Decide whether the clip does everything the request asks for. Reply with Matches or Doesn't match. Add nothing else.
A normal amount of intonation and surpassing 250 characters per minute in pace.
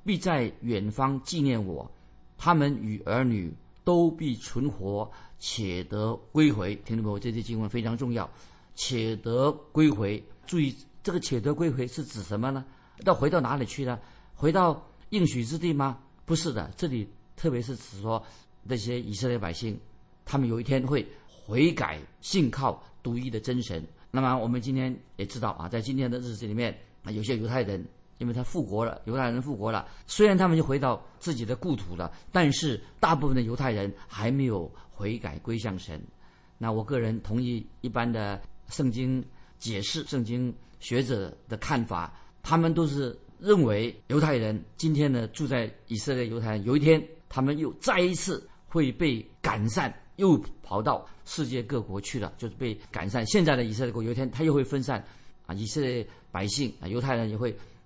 Matches